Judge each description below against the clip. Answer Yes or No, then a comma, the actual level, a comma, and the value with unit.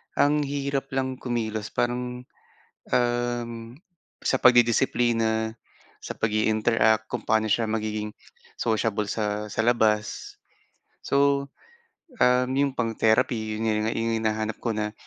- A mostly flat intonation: Yes, narrow, 2.2 semitones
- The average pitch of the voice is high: No, low, 115 Hz